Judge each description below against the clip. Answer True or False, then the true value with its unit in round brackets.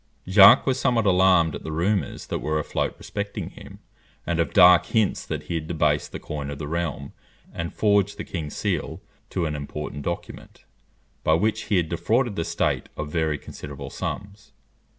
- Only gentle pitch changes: False (4.5 semitones)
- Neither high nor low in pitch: False (85 Hz)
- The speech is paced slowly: False (180 wpm)